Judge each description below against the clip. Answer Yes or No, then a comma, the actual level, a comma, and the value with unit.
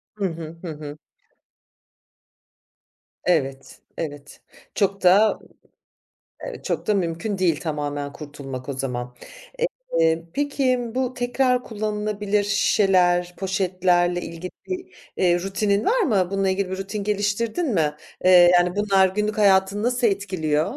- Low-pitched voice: No, high, 190 Hz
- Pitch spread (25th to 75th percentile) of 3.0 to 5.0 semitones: Yes, average, 4.0 semitones